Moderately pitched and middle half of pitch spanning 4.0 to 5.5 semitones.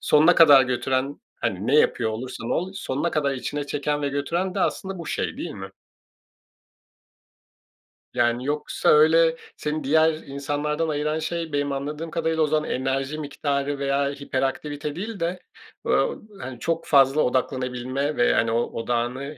No: medium, 145 Hz; average, 2.9 semitones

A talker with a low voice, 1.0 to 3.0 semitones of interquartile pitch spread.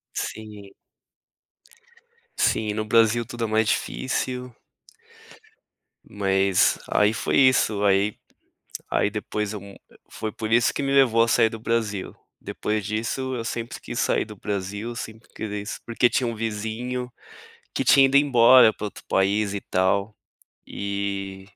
Yes: low, 110 Hz; narrow, 2.5 semitones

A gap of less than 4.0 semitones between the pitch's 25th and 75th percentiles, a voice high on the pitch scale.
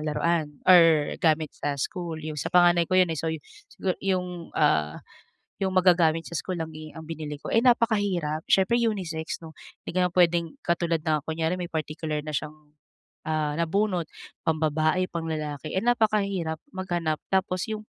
No: average, 2.9 semitones; medium, 165 Hz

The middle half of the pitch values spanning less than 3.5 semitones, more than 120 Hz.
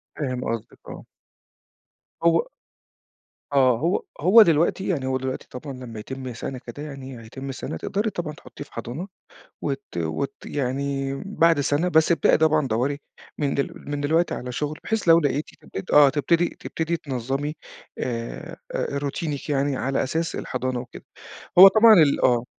No: average, 3.8 semitones; medium, 140 Hz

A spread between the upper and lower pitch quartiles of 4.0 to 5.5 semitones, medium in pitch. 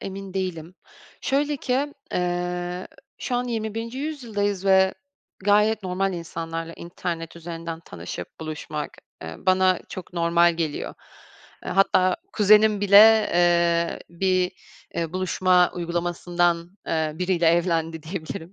No: average, 2.8 semitones; medium, 180 Hz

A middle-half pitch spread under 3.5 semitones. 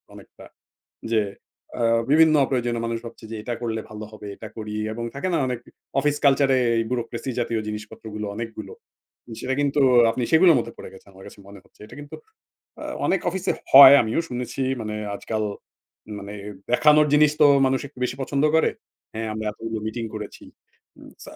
No: average, 4.2 semitones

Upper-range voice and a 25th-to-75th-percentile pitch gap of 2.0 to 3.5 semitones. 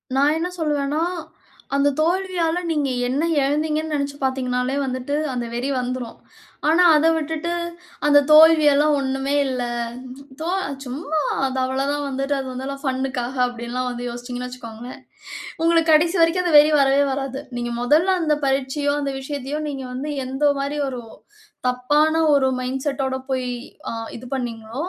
Yes: very high, 275 Hz; average, 3.0 semitones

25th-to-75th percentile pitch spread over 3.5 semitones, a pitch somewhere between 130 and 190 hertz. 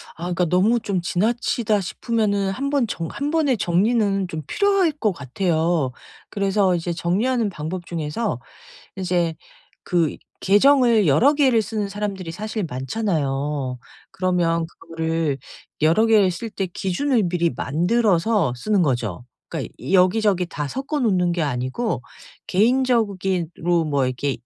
Yes: average, 5.3 semitones; medium, 185 Hz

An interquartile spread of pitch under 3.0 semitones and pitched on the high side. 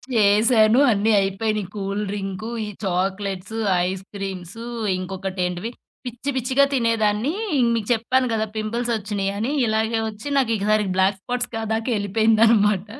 Yes: narrow, 2.6 semitones; high, 215 Hz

